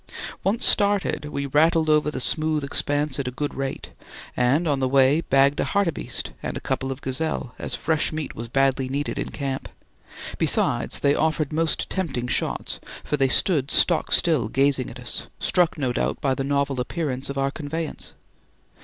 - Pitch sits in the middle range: Yes, medium, 145 Hz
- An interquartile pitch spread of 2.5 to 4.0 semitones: Yes, average, 2.8 semitones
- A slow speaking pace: No, average, 180 wpm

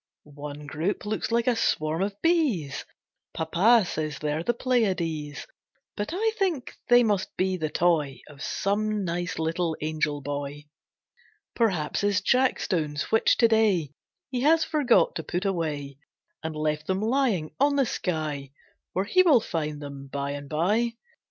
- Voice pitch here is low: No, medium, 175 Hz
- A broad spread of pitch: Yes, wide, 6.9 semitones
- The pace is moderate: Yes, average, 150 wpm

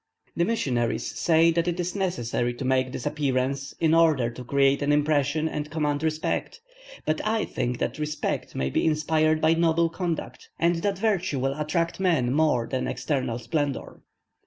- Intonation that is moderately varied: Yes, average, 3.8 semitones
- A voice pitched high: No, medium, 150 Hz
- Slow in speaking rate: No, average, 170 wpm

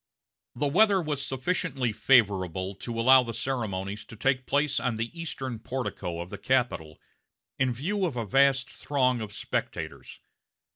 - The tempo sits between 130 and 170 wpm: Yes, average, 150 wpm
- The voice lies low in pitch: Yes, low, 125 Hz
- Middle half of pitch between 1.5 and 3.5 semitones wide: No, average, 4.1 semitones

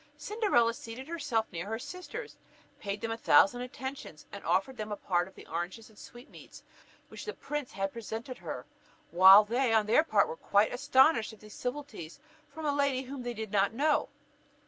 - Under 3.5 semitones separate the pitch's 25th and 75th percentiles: No, average, 5.2 semitones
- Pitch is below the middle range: No, high, 235 Hz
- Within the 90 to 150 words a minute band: No, average, 190 wpm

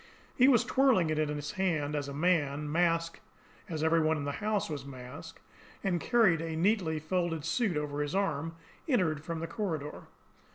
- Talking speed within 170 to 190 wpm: Yes, average, 180 wpm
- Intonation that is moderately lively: Yes, average, 3.9 semitones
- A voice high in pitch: No, medium, 165 Hz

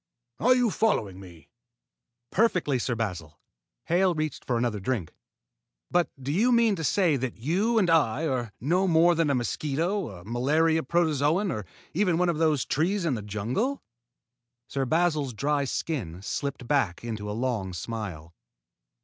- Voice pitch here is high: No, medium, 145 Hz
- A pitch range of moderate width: No, wide, 7.1 semitones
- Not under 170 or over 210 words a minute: No, average, 160 wpm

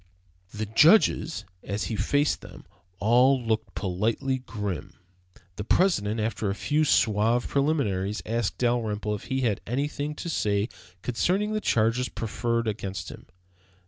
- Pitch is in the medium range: No, low, 115 Hz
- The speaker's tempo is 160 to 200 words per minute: No, slow, 135 wpm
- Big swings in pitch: No, average, 4.7 semitones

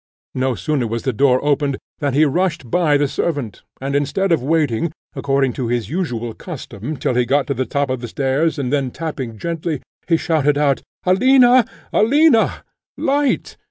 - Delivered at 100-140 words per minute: No, average, 175 wpm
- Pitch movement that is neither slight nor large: Yes, average, 4.3 semitones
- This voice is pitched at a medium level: Yes, medium, 145 Hz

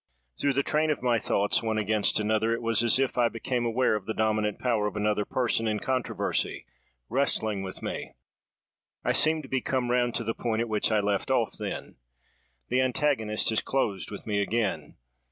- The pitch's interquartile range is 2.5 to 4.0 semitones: Yes, average, 2.9 semitones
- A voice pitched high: No, low, 115 Hz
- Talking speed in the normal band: Yes, average, 195 wpm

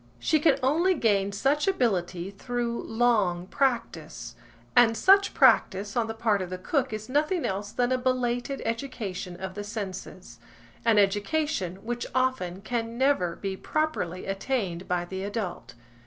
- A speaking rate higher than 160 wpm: No, average, 145 wpm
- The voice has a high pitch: Yes, high, 220 Hz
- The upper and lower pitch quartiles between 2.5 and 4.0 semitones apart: No, average, 5.3 semitones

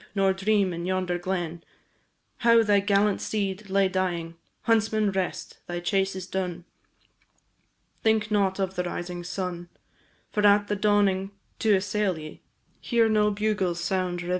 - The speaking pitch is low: No, high, 190 Hz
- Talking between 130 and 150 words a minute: Yes, average, 140 wpm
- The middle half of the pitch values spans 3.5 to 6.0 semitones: No, narrow, 2.6 semitones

